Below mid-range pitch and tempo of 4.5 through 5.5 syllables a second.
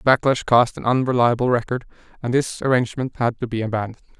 No: low, 120 Hz; 6.6 syllables/s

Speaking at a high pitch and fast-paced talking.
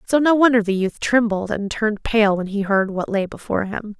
Yes: high, 210 Hz; fast, 240 wpm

